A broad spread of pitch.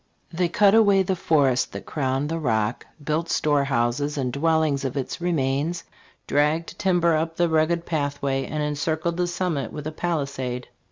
No: average, 3.5 semitones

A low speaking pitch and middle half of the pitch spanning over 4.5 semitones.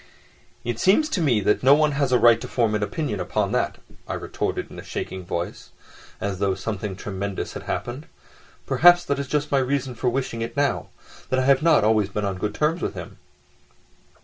Yes: low, 120 Hz; wide, 5.5 semitones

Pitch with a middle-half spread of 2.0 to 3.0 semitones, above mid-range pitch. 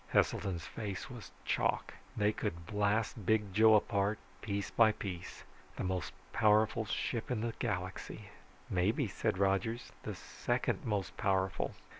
No: narrow, 2.5 semitones; low, 105 Hz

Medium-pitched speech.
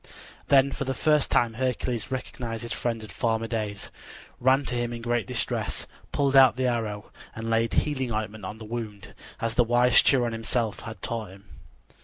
No: low, 115 Hz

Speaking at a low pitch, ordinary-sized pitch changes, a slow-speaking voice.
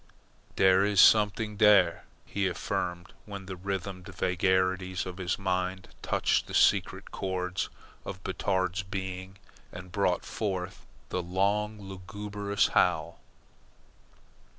No: very low, 95 Hz; narrow, 1.5 semitones; slow, 110 wpm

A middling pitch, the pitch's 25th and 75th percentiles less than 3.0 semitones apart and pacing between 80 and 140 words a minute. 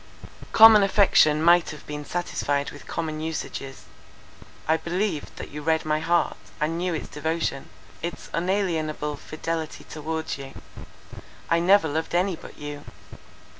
Yes: medium, 160 Hz; narrow, 2.5 semitones; slow, 135 wpm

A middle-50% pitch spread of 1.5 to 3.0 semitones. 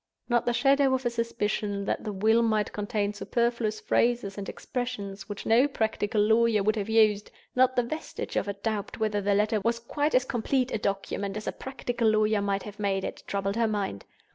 Yes: average, 2.7 semitones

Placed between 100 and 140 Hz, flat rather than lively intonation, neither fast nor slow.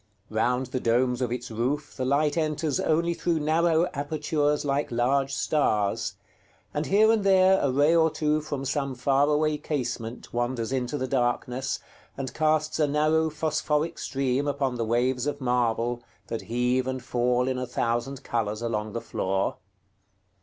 No: low, 135 Hz; average, 3.7 semitones; average, 160 wpm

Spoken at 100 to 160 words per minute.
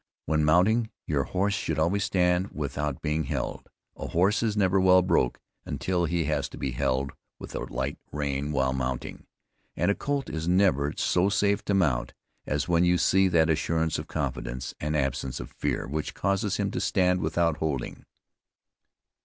No: average, 175 wpm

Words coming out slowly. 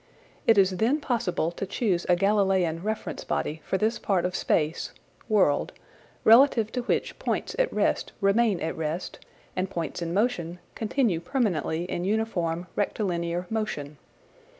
No: average, 145 wpm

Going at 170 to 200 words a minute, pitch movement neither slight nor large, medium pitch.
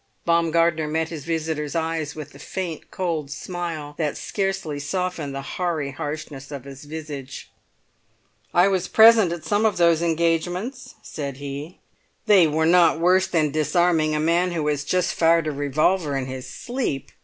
No: average, 160 wpm; average, 3.0 semitones; medium, 160 Hz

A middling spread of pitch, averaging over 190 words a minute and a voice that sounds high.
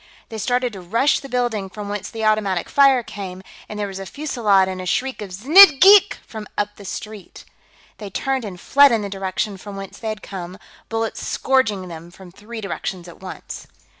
Yes: average, 4.0 semitones; average, 200 wpm; high, 210 Hz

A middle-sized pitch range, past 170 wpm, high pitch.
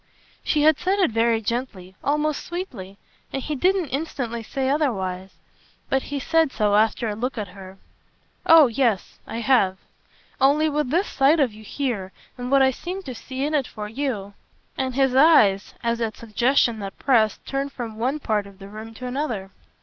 Yes: average, 4.9 semitones; average, 190 wpm; very high, 250 Hz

